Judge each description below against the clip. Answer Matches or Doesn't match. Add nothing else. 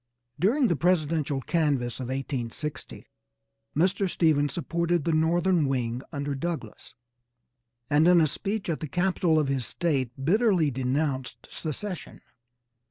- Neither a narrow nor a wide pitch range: Matches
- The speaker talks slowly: Matches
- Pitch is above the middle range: Doesn't match